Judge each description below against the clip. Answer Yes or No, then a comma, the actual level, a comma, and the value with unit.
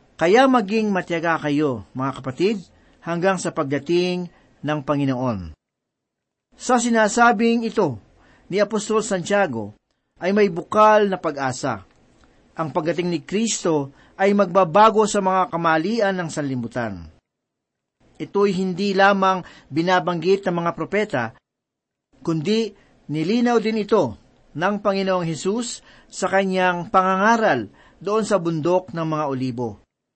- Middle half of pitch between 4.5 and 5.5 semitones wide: Yes, average, 4.8 semitones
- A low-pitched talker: No, medium, 185 Hz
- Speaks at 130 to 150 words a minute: No, slow, 110 wpm